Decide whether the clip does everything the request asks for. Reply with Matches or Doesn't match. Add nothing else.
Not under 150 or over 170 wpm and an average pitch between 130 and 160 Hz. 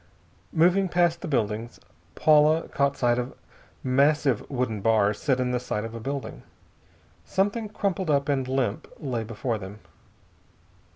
Doesn't match